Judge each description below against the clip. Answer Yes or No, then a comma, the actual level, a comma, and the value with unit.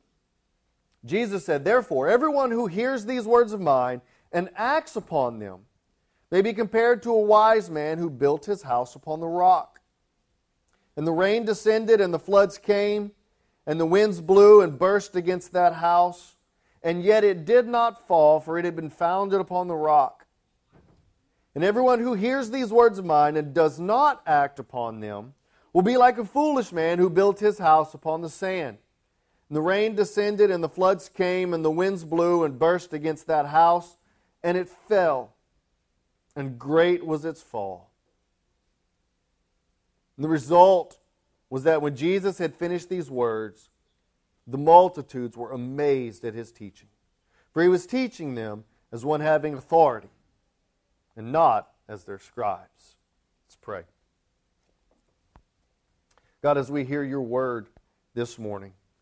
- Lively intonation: Yes, wide, 8.3 semitones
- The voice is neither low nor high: Yes, medium, 165 Hz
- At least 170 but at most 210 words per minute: No, average, 155 wpm